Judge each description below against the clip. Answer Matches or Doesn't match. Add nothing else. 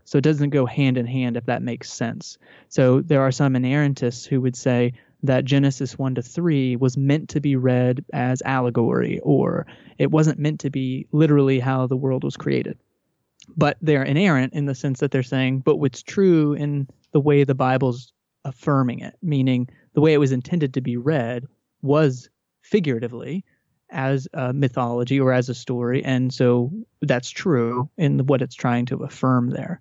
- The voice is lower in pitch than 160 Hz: Matches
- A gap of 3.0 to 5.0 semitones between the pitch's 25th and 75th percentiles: Doesn't match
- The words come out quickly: Doesn't match